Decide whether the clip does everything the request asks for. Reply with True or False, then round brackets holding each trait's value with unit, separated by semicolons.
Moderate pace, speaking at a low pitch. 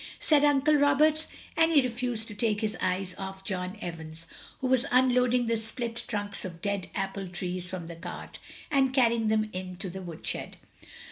False (180 wpm; 215 Hz)